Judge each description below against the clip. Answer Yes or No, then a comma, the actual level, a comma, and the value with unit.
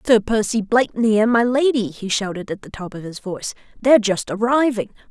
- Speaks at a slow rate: No, average, 200 wpm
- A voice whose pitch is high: Yes, high, 220 Hz